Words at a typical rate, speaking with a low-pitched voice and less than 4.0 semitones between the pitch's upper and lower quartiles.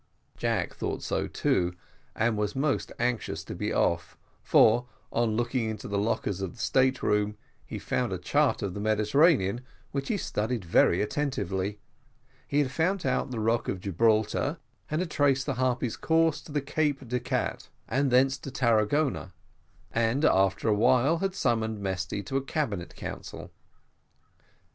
No: average, 165 wpm; low, 120 Hz; average, 4.8 semitones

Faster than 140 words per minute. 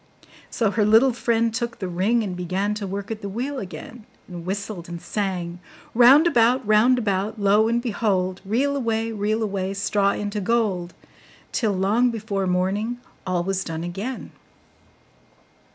Yes: average, 155 wpm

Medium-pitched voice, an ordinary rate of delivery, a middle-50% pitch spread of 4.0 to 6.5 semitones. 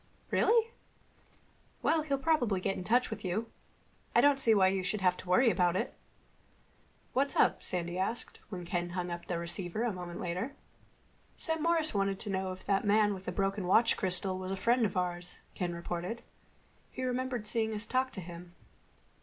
No: high, 195 Hz; average, 185 wpm; average, 4.9 semitones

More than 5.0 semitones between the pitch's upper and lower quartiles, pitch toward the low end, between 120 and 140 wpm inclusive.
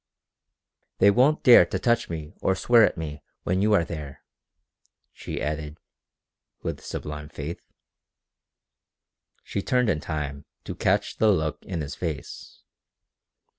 Yes: wide, 5.4 semitones; very low, 80 Hz; slow, 135 wpm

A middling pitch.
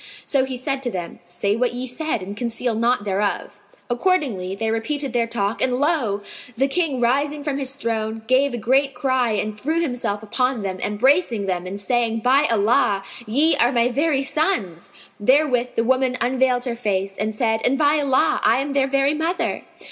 No: high, 245 Hz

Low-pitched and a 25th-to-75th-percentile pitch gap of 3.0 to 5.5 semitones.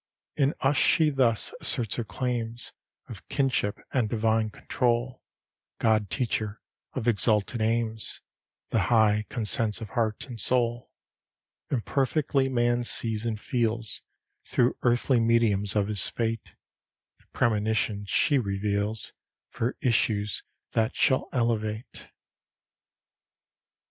No: low, 115 Hz; narrow, 2.4 semitones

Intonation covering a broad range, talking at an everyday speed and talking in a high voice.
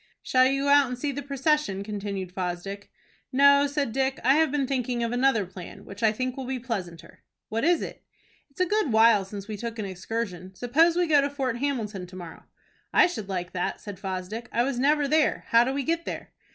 No: wide, 5.9 semitones; fast, 220 wpm; high, 245 Hz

